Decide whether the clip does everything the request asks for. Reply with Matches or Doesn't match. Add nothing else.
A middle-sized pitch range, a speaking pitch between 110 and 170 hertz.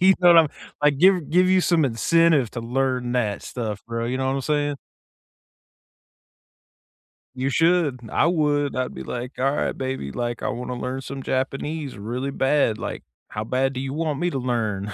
Matches